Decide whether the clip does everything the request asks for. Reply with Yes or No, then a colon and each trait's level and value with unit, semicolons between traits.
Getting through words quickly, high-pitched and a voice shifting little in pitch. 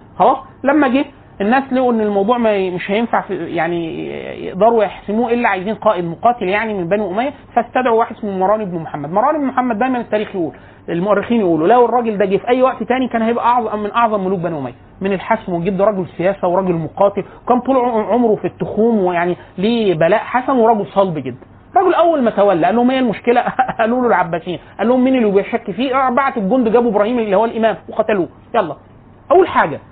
No: fast, 200 wpm; high, 215 Hz; average, 4.1 semitones